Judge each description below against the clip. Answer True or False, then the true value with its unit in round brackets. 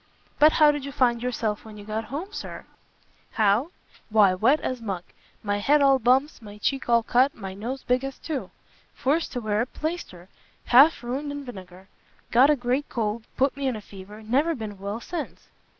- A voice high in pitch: True (245 Hz)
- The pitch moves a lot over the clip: False (4.7 semitones)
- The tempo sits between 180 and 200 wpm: True (195 wpm)